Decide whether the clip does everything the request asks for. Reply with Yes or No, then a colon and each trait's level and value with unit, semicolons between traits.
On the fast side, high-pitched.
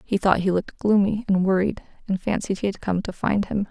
Yes: fast, 245 wpm; high, 195 Hz